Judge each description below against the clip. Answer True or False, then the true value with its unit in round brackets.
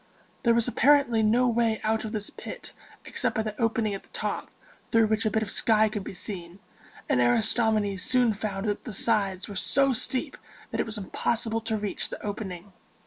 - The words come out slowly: False (195 wpm)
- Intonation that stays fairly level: True (2.1 semitones)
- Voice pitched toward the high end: True (220 Hz)